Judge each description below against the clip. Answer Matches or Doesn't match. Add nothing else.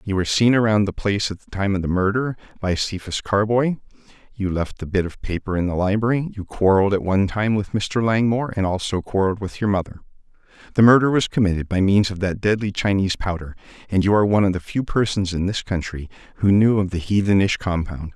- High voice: Doesn't match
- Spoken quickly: Matches